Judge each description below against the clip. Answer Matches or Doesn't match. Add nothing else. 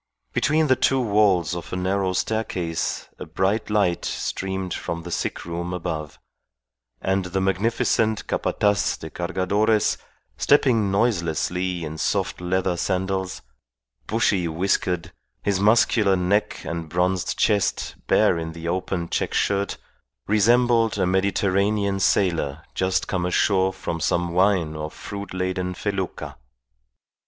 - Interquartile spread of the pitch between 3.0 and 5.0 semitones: Doesn't match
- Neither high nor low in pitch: Doesn't match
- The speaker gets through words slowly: Matches